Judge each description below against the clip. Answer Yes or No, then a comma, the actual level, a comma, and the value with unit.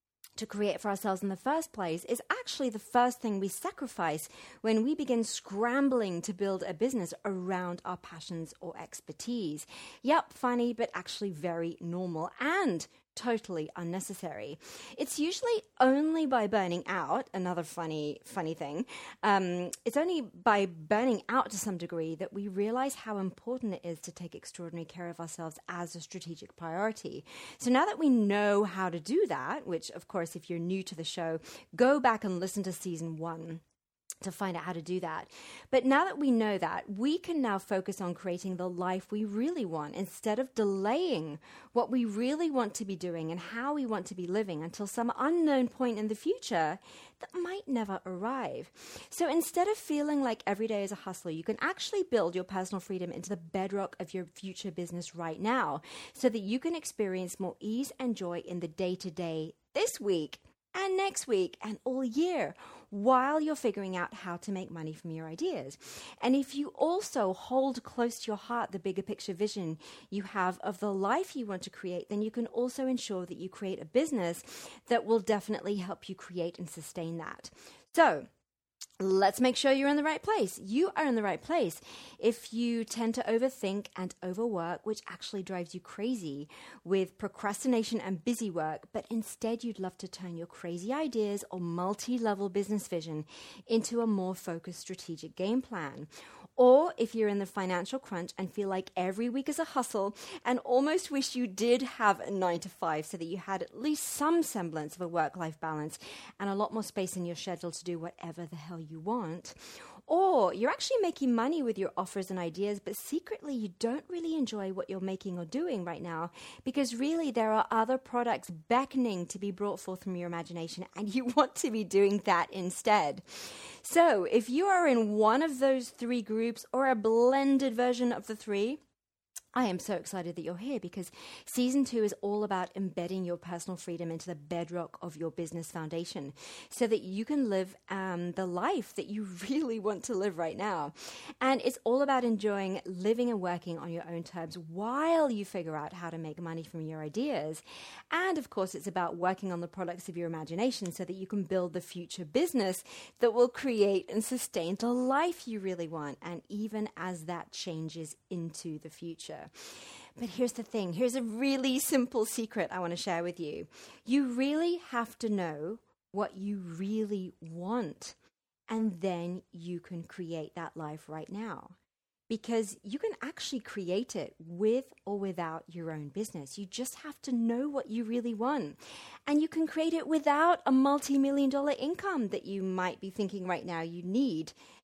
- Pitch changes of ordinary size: No, wide, 5.9 semitones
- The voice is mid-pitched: No, high, 205 Hz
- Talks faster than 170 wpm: Yes, average, 190 wpm